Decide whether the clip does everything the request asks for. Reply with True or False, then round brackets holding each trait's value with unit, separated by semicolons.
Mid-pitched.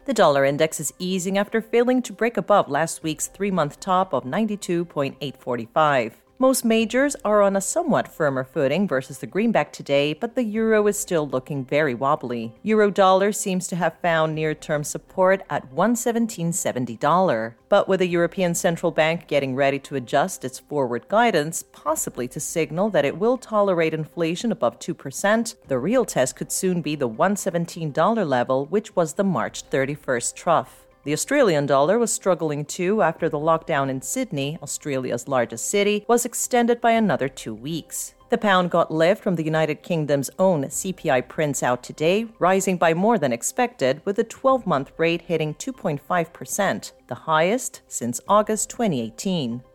True (170 Hz)